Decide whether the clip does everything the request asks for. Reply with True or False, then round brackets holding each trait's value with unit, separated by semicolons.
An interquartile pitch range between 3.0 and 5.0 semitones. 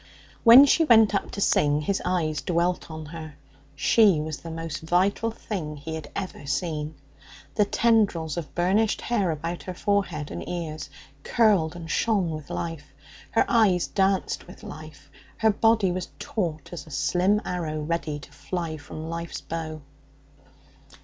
True (4.3 semitones)